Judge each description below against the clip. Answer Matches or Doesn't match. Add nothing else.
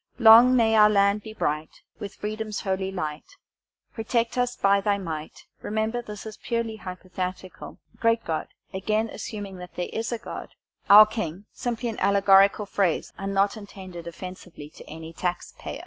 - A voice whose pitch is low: Doesn't match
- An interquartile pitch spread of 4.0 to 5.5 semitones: Doesn't match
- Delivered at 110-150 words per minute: Doesn't match